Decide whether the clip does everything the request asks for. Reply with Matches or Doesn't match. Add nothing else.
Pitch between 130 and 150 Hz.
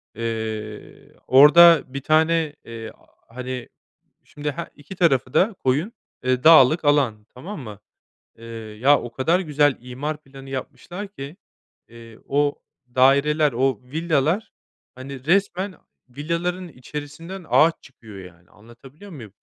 Matches